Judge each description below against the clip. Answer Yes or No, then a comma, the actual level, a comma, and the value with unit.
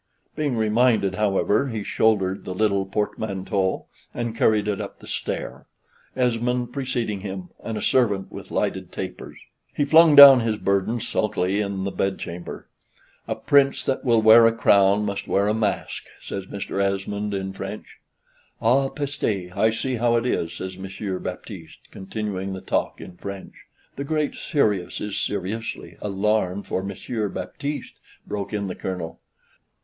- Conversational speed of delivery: Yes, average, 155 wpm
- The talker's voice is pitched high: No, low, 105 Hz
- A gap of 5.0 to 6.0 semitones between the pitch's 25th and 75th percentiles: No, average, 3.4 semitones